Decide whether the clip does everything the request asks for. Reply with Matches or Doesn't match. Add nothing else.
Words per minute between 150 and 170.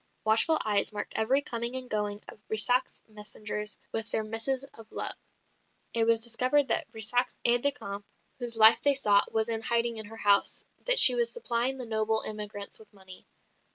Doesn't match